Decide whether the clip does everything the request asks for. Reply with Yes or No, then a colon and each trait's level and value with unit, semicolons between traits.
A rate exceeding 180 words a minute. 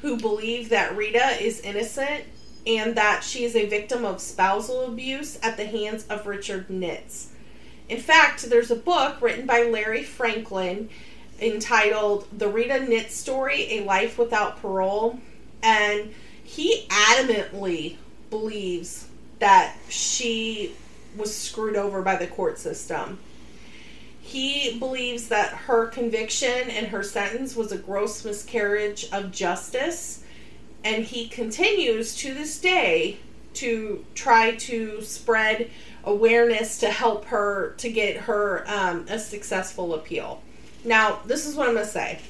No: slow, 135 wpm